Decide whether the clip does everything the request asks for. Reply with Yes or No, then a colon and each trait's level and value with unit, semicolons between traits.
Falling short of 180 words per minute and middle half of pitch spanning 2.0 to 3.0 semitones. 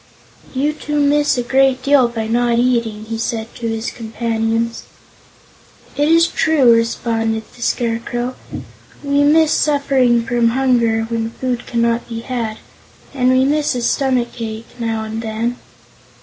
Yes: average, 140 wpm; narrow, 2.6 semitones